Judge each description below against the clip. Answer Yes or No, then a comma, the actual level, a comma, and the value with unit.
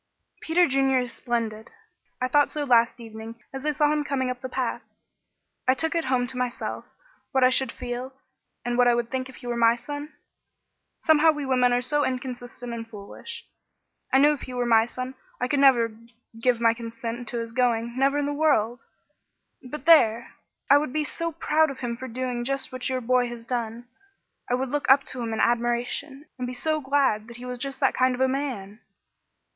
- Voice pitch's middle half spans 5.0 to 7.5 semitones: No, narrow, 2.5 semitones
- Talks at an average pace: No, fast, 210 wpm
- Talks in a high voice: Yes, very high, 250 Hz